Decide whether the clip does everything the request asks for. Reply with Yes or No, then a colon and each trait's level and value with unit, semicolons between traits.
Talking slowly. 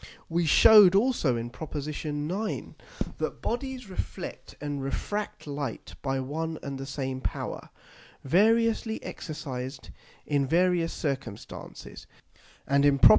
Yes: slow, 120 wpm